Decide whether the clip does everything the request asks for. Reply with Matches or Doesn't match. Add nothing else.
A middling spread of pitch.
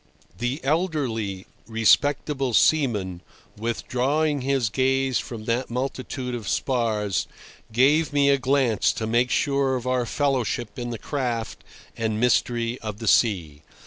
Matches